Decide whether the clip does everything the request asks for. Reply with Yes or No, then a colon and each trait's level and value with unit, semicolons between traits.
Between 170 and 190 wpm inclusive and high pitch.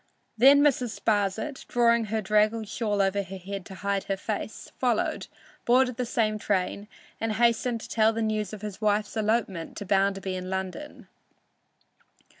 No: average, 160 wpm; high, 215 Hz